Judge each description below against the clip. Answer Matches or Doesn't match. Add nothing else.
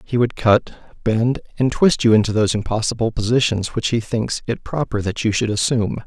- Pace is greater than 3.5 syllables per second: Matches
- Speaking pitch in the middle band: Doesn't match